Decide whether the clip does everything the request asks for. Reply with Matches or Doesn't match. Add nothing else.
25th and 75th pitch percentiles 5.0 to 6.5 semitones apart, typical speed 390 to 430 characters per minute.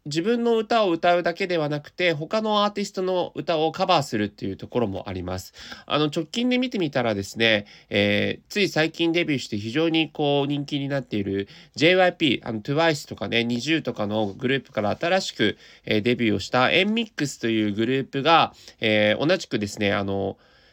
Doesn't match